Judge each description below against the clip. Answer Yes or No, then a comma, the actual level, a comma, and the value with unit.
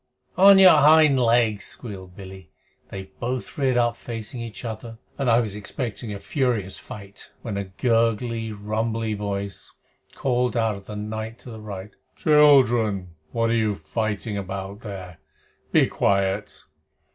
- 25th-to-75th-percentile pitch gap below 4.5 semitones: Yes, average, 3.2 semitones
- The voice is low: Yes, low, 110 Hz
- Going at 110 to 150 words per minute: Yes, average, 145 wpm